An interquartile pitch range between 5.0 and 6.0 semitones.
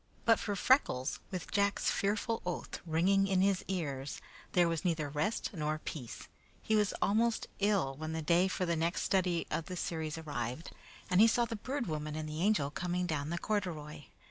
No: average, 4.5 semitones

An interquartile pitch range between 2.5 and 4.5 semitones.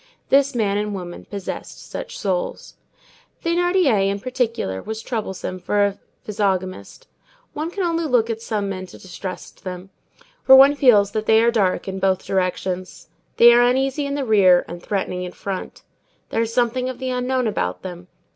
No: average, 5.3 semitones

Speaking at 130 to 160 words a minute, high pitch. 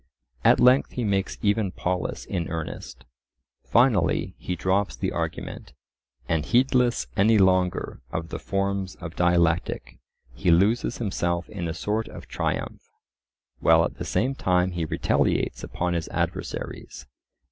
No: slow, 135 wpm; very low, 95 Hz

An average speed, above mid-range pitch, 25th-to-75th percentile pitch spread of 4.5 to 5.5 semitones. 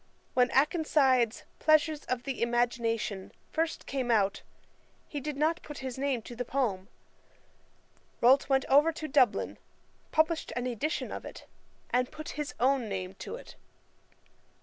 No: average, 145 wpm; very high, 265 Hz; average, 4.0 semitones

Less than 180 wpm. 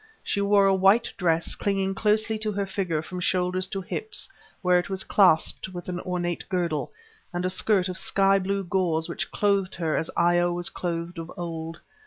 No: average, 190 wpm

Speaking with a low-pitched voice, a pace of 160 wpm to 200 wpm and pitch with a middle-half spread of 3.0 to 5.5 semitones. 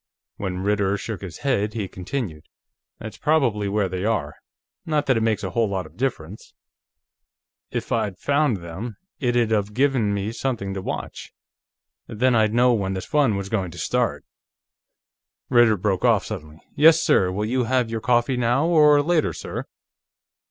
Yes: low, 110 Hz; average, 165 wpm; average, 4.4 semitones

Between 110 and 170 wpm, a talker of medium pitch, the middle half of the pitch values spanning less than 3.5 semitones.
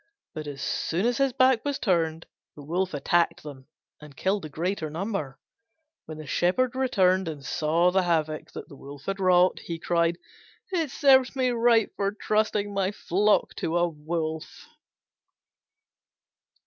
No: average, 150 wpm; medium, 180 Hz; average, 5.1 semitones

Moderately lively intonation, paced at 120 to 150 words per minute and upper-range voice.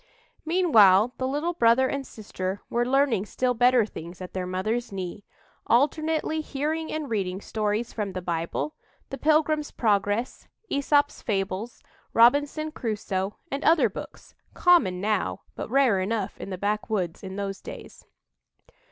No: wide, 6.4 semitones; average, 140 wpm; high, 230 Hz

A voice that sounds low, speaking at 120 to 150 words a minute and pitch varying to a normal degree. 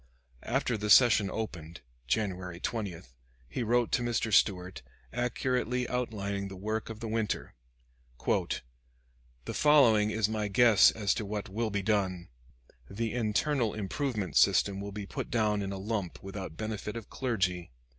Yes: low, 105 Hz; average, 145 wpm; average, 3.0 semitones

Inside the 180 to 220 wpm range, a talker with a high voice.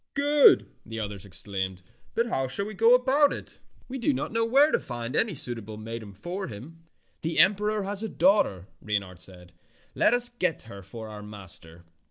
No: average, 190 wpm; low, 130 Hz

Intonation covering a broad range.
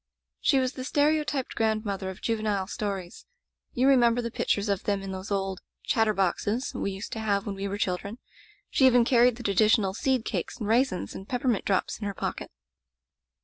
No: average, 3.8 semitones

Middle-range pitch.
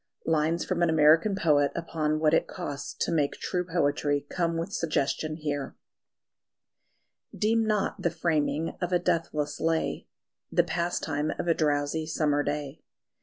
Yes: medium, 160 Hz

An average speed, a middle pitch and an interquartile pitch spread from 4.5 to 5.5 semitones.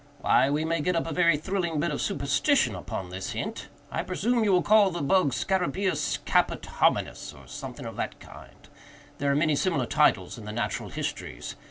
Yes: average, 190 wpm; medium, 160 Hz; average, 5.1 semitones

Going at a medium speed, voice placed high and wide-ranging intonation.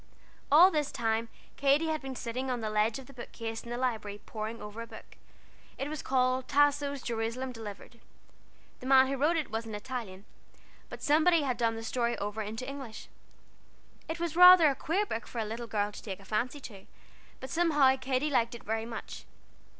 No: average, 195 wpm; very high, 250 Hz; average, 4.0 semitones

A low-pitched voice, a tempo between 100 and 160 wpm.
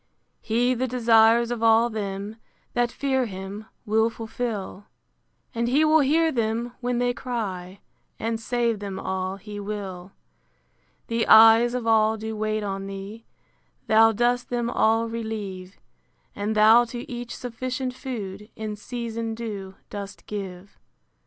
No: high, 225 Hz; average, 140 wpm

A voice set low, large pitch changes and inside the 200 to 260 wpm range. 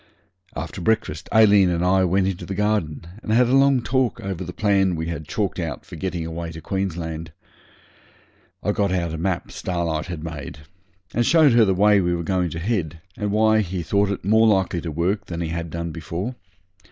No: very low, 90 Hz; average, 3.8 semitones; fast, 205 wpm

